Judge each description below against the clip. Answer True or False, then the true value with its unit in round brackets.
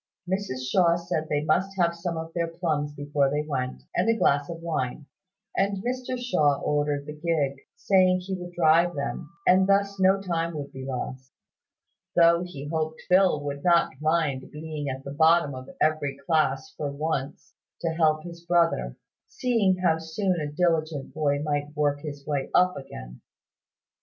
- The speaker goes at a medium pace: True (170 wpm)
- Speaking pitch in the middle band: True (155 Hz)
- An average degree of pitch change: True (3.4 semitones)